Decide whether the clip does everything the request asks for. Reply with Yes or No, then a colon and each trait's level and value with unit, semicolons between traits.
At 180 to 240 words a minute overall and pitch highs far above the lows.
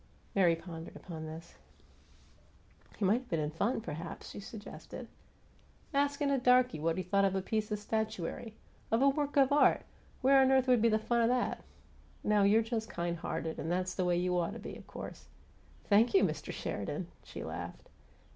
Yes: average, 195 wpm; wide, 6.1 semitones